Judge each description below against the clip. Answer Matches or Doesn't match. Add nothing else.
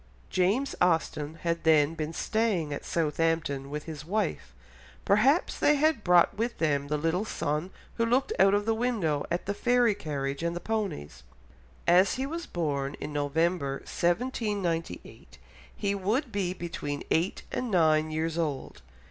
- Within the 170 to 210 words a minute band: Doesn't match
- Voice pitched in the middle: Matches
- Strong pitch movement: Matches